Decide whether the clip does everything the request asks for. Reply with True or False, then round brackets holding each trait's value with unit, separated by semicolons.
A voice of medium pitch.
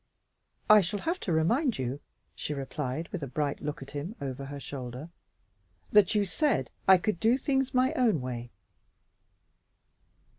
True (165 Hz)